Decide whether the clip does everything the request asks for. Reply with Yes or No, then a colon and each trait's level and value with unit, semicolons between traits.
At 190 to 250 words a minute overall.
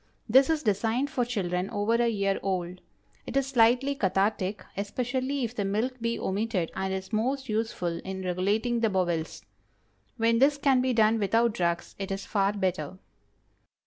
No: average, 165 wpm